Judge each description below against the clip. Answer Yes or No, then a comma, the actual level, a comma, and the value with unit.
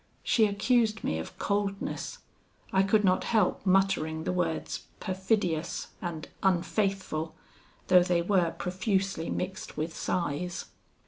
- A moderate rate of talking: No, slow, 120 wpm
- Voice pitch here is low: No, medium, 185 Hz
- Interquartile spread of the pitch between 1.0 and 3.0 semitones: Yes, average, 2.7 semitones